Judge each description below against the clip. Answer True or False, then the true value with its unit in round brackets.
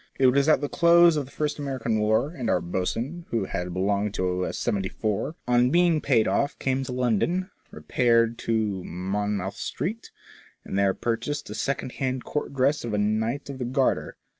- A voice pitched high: False (120 Hz)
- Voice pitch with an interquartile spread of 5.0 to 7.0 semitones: True (5.3 semitones)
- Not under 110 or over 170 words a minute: False (190 wpm)